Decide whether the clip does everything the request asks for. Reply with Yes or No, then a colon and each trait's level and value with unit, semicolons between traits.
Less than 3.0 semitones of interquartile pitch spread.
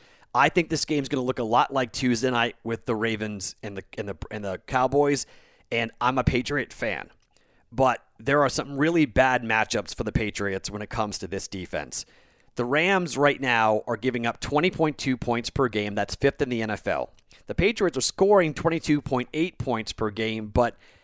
No: average, 4.5 semitones